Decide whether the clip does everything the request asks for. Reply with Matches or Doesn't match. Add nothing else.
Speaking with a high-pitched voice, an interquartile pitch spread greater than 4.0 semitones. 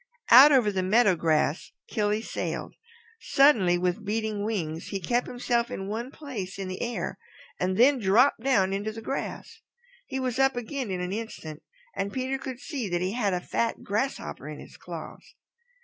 Matches